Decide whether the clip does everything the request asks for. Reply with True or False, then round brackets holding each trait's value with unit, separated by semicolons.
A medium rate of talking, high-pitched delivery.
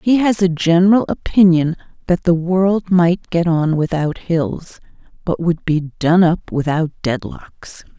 False (150 wpm; 170 Hz)